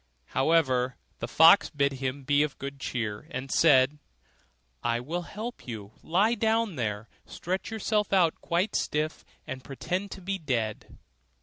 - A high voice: No, medium, 150 Hz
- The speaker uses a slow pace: No, average, 145 wpm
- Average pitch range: No, wide, 6.3 semitones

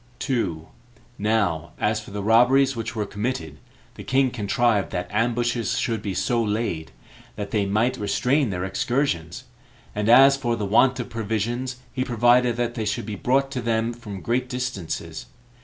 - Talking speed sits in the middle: Yes, average, 165 wpm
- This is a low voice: Yes, low, 115 Hz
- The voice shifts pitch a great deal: No, average, 3.3 semitones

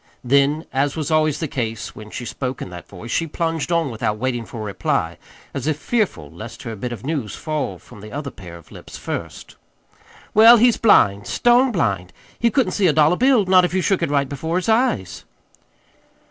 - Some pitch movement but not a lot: No, wide, 8.4 semitones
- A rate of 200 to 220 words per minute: Yes, fast, 205 wpm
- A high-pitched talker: No, medium, 140 Hz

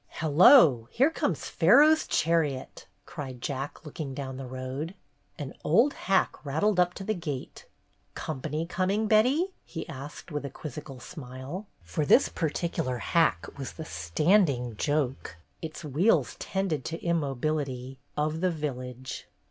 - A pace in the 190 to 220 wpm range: No, average, 150 wpm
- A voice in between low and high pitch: Yes, medium, 150 Hz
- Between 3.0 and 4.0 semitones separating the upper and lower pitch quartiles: No, average, 5.0 semitones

